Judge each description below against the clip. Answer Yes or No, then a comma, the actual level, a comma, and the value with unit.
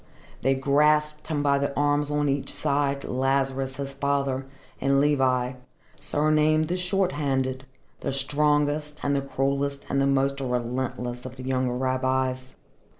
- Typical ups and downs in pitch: No, narrow, 1.8 semitones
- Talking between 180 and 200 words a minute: No, average, 145 wpm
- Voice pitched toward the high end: No, medium, 140 Hz